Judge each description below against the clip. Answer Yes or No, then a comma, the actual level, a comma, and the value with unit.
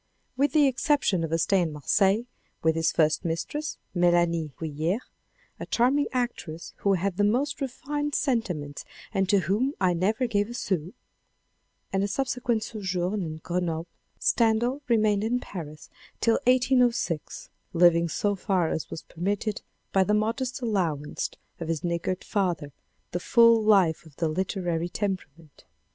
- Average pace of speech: Yes, average, 150 wpm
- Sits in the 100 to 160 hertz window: No, high, 195 Hz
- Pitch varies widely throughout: Yes, wide, 5.7 semitones